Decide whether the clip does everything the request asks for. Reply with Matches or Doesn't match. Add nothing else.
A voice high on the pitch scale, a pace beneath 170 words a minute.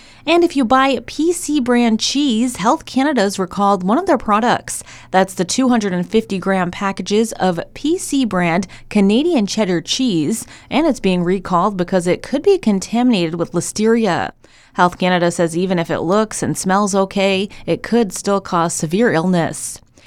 Matches